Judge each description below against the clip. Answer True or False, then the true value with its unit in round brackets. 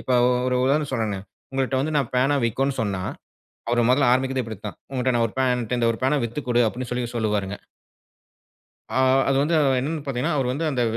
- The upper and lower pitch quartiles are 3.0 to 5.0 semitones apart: False (2.6 semitones)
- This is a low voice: True (125 Hz)